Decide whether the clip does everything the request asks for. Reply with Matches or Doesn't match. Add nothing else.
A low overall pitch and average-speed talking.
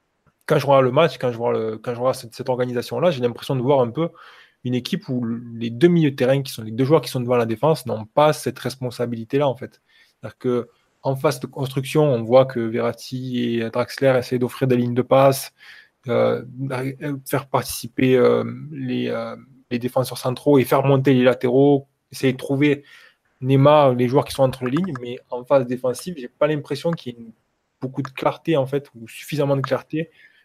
Matches